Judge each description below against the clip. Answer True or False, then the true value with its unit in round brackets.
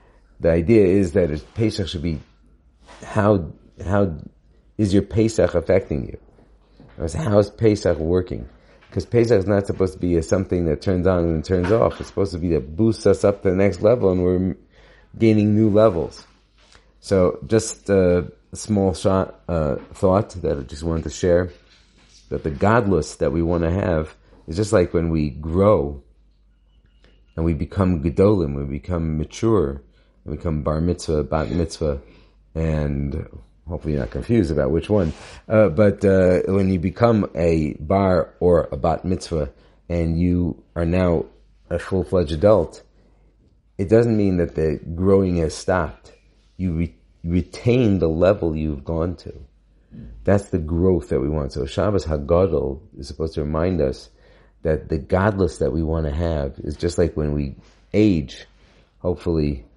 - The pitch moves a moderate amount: True (3.8 semitones)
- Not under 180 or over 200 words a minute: False (165 wpm)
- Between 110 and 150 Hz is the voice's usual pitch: False (85 Hz)